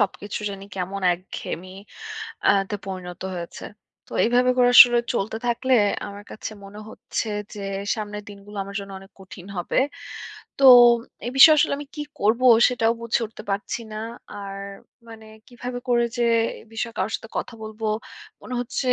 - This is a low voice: No, high, 215 Hz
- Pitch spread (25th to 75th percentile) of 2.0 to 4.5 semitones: Yes, average, 3.4 semitones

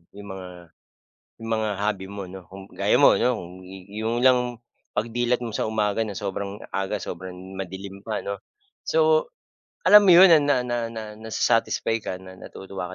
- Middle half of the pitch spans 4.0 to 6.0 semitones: No, average, 3.5 semitones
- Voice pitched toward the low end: Yes, low, 105 Hz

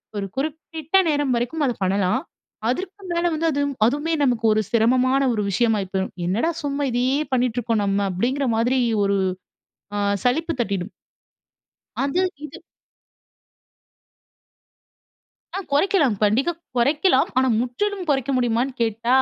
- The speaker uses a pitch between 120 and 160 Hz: No, very high, 255 Hz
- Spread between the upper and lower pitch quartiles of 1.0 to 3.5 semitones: No, average, 4.6 semitones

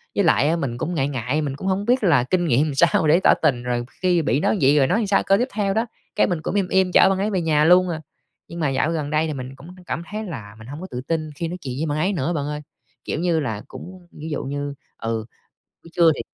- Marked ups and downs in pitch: No, average, 4.7 semitones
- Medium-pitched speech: Yes, medium, 160 Hz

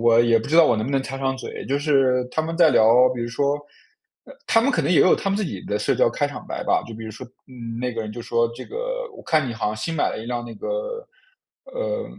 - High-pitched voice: No, low, 130 Hz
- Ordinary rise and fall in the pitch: No, wide, 6.1 semitones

